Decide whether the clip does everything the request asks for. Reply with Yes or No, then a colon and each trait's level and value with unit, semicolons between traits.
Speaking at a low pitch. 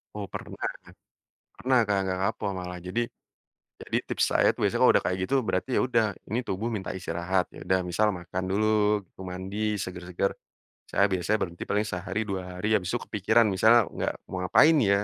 Yes: very low, 95 Hz